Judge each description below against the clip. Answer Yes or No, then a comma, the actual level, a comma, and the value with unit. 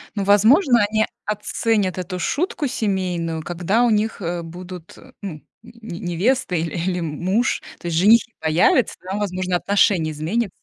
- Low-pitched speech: No, medium, 185 Hz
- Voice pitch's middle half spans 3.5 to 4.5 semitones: Yes, average, 4.1 semitones